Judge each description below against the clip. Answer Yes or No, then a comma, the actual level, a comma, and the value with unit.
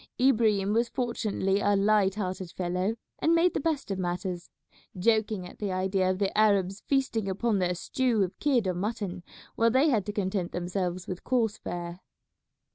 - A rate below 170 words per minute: No, average, 175 wpm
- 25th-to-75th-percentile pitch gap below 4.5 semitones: Yes, average, 3.5 semitones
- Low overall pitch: No, high, 200 Hz